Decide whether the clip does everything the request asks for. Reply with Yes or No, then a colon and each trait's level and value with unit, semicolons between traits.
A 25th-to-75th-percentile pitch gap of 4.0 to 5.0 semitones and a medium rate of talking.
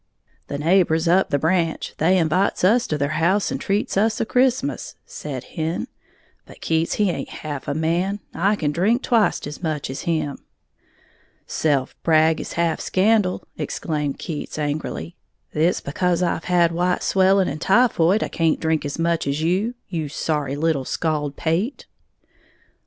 No: average, 3.6 semitones; average, 160 wpm